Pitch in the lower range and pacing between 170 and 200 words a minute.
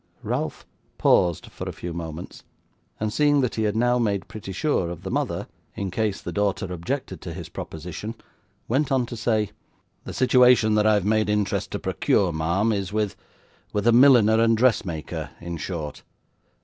Yes: low, 105 Hz; average, 175 wpm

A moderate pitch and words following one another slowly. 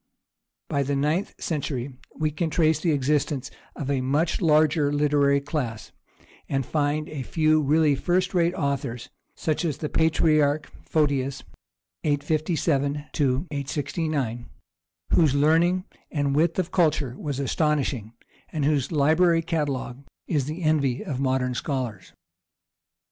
Yes: medium, 145 Hz; slow, 125 wpm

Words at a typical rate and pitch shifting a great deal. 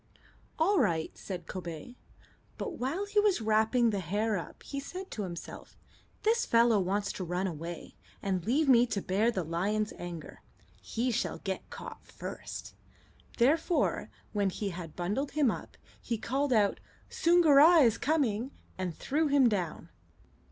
Yes: average, 150 wpm; wide, 7.1 semitones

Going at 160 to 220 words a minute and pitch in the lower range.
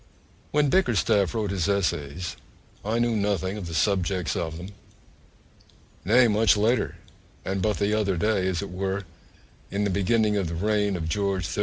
Yes: average, 170 wpm; low, 100 Hz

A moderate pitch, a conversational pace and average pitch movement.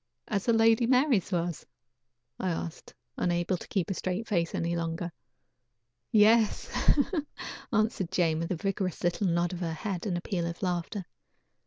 Yes: medium, 180 Hz; average, 160 wpm; average, 3.5 semitones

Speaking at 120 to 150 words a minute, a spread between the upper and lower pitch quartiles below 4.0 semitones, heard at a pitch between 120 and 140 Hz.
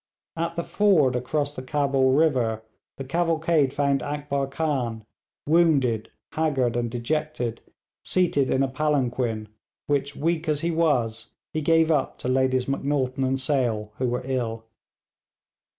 Yes: slow, 135 wpm; average, 3.6 semitones; low, 135 Hz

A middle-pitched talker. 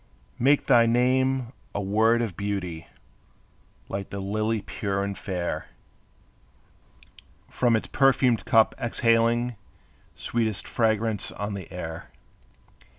No: low, 110 Hz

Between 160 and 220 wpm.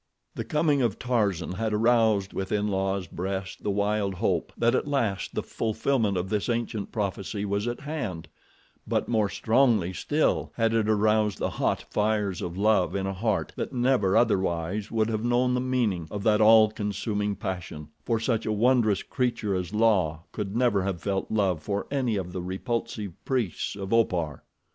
Yes: average, 175 wpm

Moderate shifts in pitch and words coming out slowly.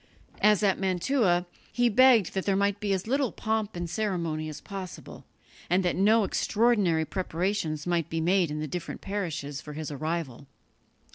No: average, 4.3 semitones; average, 165 wpm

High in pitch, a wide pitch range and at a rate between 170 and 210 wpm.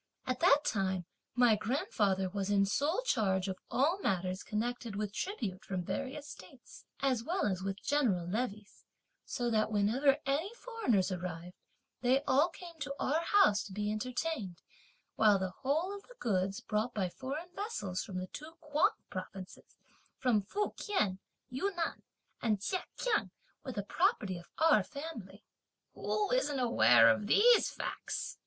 No: high, 230 Hz; wide, 7.3 semitones; average, 150 wpm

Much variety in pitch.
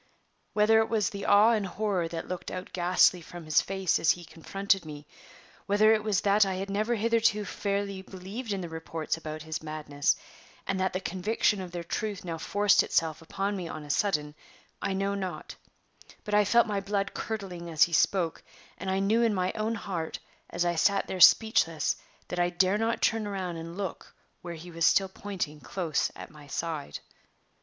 No: average, 3.5 semitones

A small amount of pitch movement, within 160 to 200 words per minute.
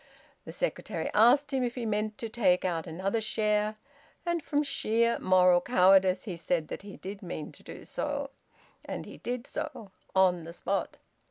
No: average, 4.2 semitones; average, 175 wpm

